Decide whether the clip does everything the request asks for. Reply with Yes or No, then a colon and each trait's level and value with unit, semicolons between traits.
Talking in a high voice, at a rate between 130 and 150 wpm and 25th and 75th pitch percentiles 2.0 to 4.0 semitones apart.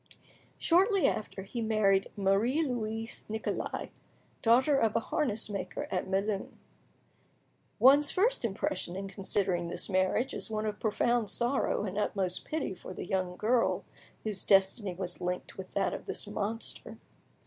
Yes: high, 210 Hz; average, 145 wpm; average, 3.6 semitones